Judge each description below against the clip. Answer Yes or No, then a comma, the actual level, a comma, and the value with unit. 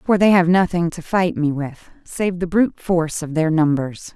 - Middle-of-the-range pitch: Yes, medium, 170 Hz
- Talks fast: Yes, fast, 215 wpm